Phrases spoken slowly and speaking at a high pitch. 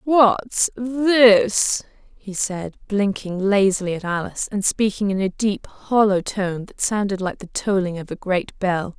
No: average, 160 wpm; high, 200 Hz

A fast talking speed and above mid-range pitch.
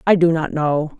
No: fast, 240 wpm; medium, 160 Hz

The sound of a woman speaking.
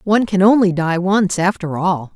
Yes: female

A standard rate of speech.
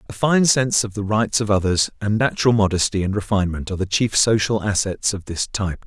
No: fast, 215 wpm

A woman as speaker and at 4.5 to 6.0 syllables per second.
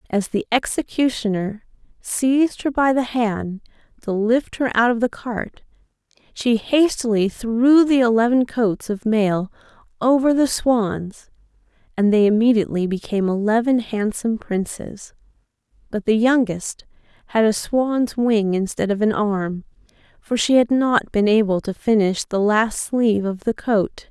No: female; 4.3 syllables/s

